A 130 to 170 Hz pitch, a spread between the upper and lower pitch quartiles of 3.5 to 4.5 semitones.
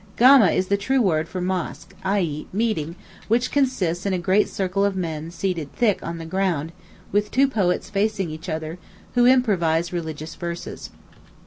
No: medium, 185 Hz; average, 4.0 semitones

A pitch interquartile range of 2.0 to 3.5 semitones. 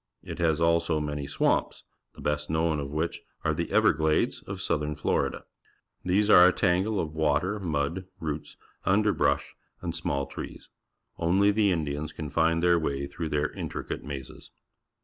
Yes: average, 3.1 semitones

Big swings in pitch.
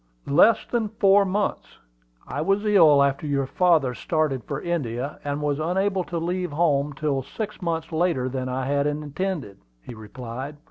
No: average, 4.7 semitones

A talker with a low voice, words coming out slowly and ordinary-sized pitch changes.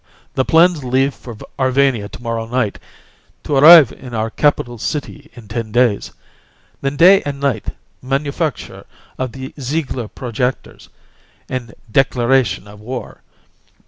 Yes: low, 130 Hz; slow, 130 wpm; average, 3.1 semitones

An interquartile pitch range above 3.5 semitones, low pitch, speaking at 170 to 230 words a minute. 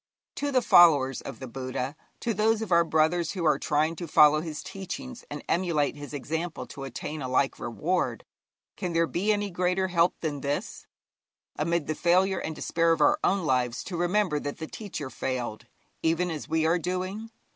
No: average, 4.0 semitones; medium, 165 Hz; average, 190 wpm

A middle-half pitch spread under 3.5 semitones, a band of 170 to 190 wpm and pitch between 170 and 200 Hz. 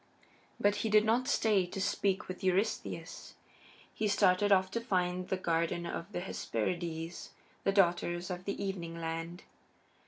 No: narrow, 2.6 semitones; average, 150 wpm; medium, 185 Hz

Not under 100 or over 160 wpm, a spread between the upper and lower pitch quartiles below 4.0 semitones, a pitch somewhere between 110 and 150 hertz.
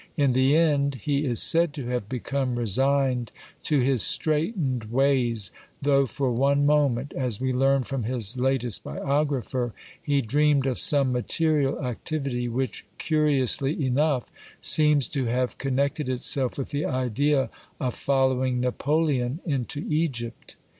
Yes: average, 140 wpm; narrow, 2.5 semitones; low, 135 Hz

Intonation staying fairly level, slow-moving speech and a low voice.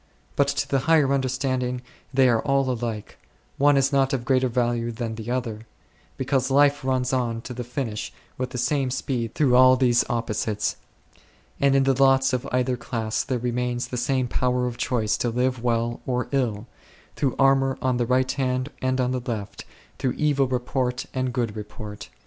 No: narrow, 1.9 semitones; average, 190 wpm; low, 125 Hz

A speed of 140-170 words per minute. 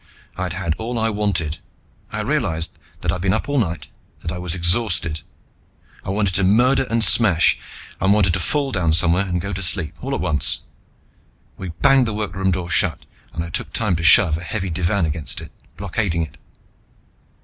No: average, 190 wpm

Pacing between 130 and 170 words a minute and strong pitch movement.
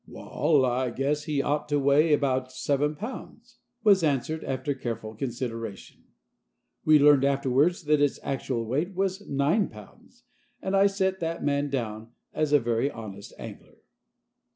No: average, 150 wpm; average, 3.6 semitones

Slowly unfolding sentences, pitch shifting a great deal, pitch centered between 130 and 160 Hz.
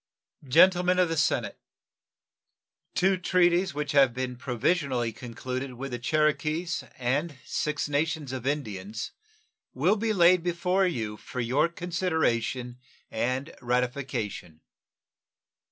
Yes: slow, 110 wpm; wide, 5.8 semitones; medium, 140 Hz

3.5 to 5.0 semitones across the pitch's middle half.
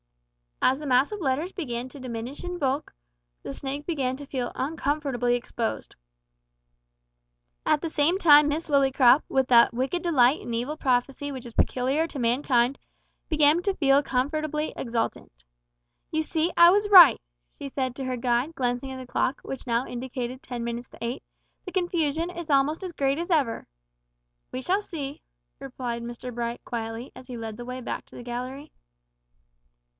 Yes: average, 3.8 semitones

